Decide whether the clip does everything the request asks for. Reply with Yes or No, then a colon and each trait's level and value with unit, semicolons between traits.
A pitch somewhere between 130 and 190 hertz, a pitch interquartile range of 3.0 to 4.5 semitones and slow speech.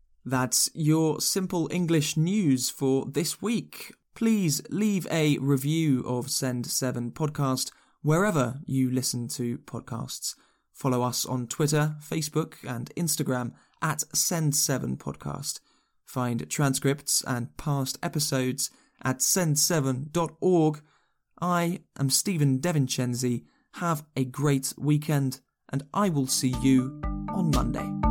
Yes: medium, 140 Hz; average, 3.4 semitones; slow, 110 wpm